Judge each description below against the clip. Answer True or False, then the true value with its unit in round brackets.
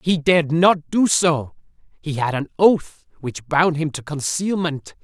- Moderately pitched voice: True (155 Hz)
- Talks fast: False (165 wpm)